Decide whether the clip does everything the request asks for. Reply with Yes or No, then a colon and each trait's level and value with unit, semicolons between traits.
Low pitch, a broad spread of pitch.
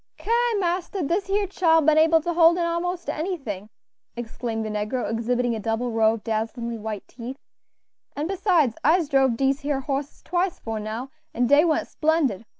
No: very high, 275 Hz; wide, 6.7 semitones